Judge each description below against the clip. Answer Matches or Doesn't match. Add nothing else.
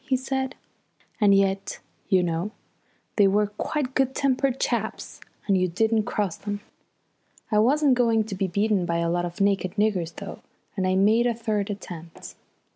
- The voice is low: Doesn't match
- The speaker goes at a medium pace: Matches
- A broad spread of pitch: Doesn't match